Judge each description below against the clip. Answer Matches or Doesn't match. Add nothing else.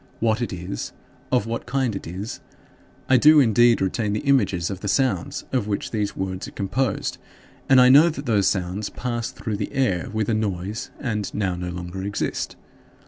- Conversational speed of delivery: Matches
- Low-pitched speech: Matches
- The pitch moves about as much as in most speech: Matches